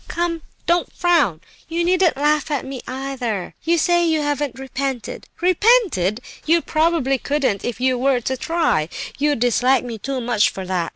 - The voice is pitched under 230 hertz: No, very high, 275 Hz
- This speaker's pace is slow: No, average, 165 wpm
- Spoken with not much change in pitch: No, average, 5.3 semitones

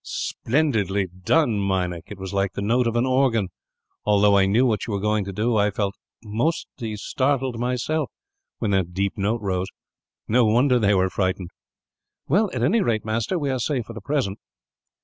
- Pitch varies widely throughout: No, average, 4.3 semitones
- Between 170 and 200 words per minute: Yes, average, 185 wpm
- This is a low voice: Yes, low, 110 Hz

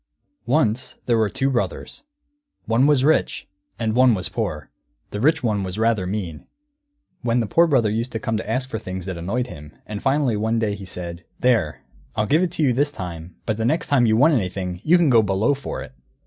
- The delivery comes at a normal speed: No, fast, 220 wpm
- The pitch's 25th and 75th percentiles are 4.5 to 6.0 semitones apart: Yes, average, 5.2 semitones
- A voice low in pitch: Yes, low, 110 Hz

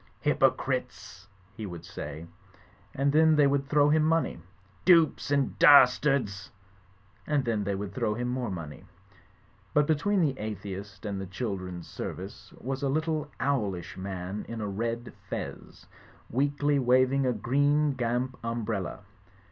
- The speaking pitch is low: Yes, low, 125 Hz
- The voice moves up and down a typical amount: No, wide, 6.1 semitones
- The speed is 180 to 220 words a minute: No, average, 145 wpm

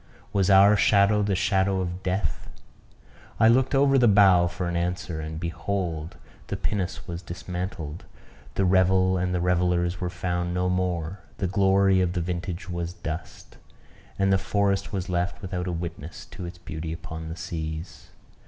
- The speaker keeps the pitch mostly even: Yes, narrow, 2.0 semitones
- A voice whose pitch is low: Yes, very low, 90 Hz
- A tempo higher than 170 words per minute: No, average, 165 wpm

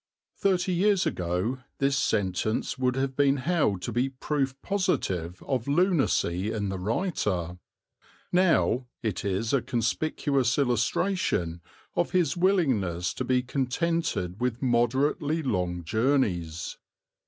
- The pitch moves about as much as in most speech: No, wide, 7.3 semitones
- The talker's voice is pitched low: Yes, low, 125 Hz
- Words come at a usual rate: No, slow, 120 wpm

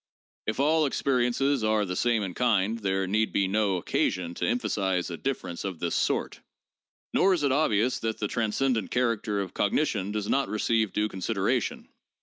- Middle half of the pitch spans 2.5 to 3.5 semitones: No, average, 4.3 semitones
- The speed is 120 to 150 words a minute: No, average, 175 wpm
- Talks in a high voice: No, low, 110 Hz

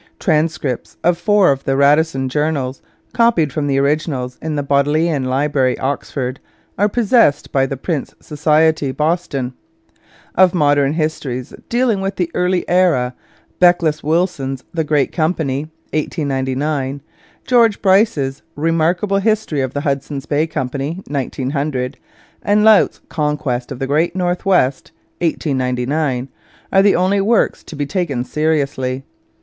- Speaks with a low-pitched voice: No, medium, 150 Hz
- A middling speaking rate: No, slow, 130 wpm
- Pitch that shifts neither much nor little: Yes, average, 4.4 semitones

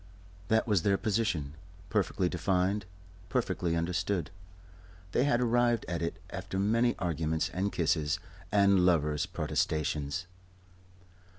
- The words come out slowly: Yes, slow, 110 wpm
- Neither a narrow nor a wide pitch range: Yes, average, 3.9 semitones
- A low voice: Yes, very low, 90 Hz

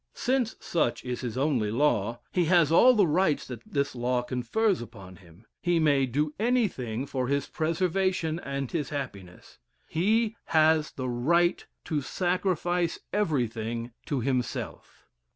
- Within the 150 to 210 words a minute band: No, average, 140 wpm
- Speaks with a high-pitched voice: No, medium, 145 Hz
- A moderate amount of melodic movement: No, wide, 6.1 semitones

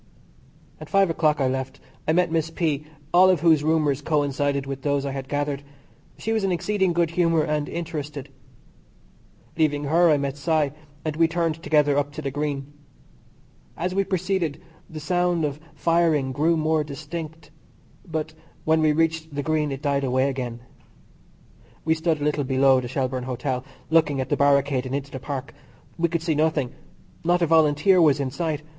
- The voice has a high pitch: No, medium, 150 Hz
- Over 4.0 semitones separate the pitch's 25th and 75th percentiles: No, average, 2.8 semitones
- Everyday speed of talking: Yes, average, 180 wpm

